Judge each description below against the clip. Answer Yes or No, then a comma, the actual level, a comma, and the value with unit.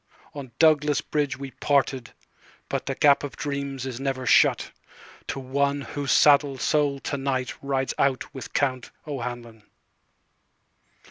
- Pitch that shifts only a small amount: Yes, narrow, 1.5 semitones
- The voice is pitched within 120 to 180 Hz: Yes, medium, 140 Hz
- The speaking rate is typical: No, slow, 120 wpm